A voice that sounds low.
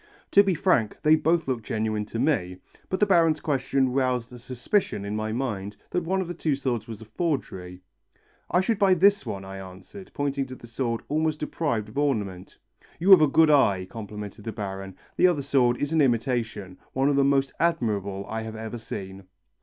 Yes: low, 125 Hz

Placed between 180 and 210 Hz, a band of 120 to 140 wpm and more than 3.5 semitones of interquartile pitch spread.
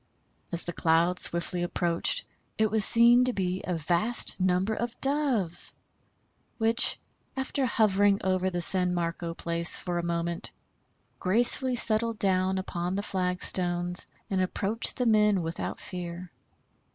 Yes: medium, 185 Hz; slow, 135 wpm; average, 3.9 semitones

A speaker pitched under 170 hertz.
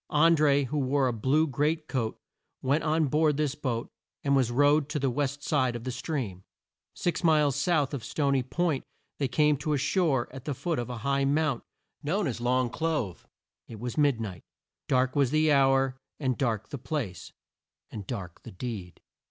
Yes: medium, 140 Hz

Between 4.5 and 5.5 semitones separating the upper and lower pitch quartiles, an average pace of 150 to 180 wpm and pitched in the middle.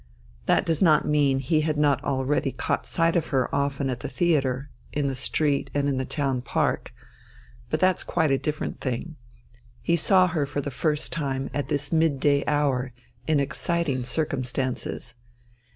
No: narrow, 2.6 semitones; average, 170 wpm; medium, 145 Hz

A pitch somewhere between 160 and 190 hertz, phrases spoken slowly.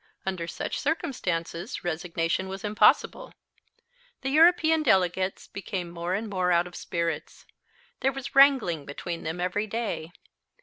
Yes: medium, 185 Hz; slow, 130 wpm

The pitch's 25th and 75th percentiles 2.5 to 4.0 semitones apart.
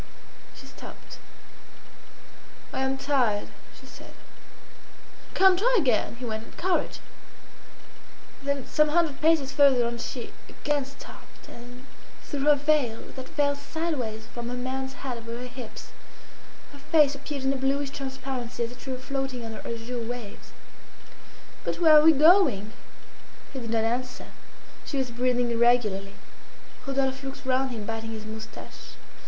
Yes: average, 3.1 semitones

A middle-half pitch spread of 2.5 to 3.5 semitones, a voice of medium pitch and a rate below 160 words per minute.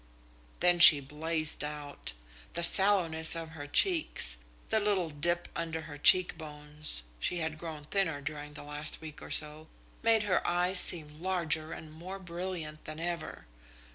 Yes: average, 2.8 semitones; medium, 160 Hz; average, 150 wpm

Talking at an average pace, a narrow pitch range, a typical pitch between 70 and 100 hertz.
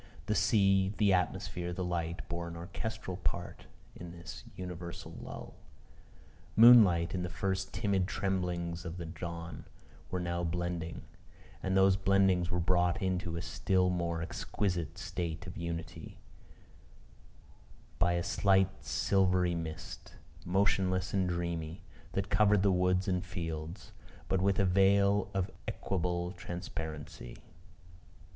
No: slow, 125 wpm; narrow, 1.9 semitones; very low, 90 Hz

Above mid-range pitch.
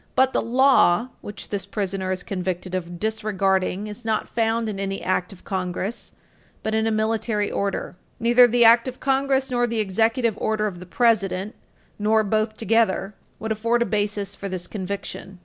Yes: high, 215 Hz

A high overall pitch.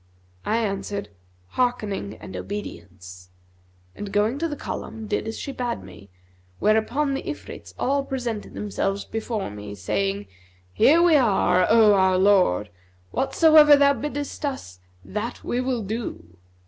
Yes: high, 215 Hz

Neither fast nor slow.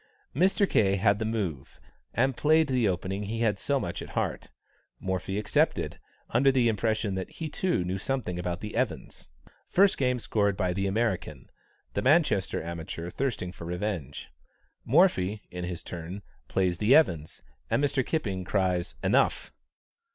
Yes: average, 155 wpm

